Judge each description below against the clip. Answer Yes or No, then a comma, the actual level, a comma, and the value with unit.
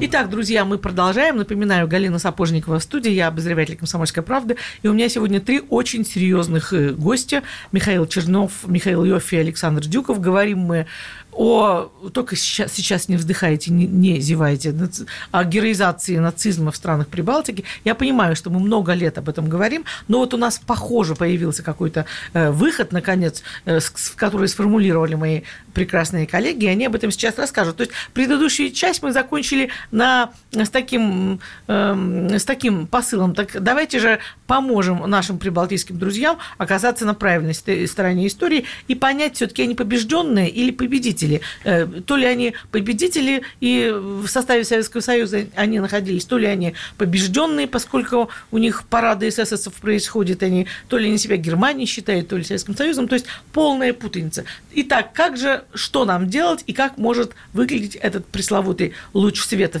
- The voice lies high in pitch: Yes, high, 205 Hz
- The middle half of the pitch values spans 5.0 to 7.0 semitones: Yes, average, 5.3 semitones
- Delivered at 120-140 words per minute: No, average, 155 wpm